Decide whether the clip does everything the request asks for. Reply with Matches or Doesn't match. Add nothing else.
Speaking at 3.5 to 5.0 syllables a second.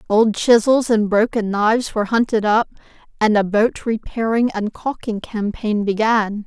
Matches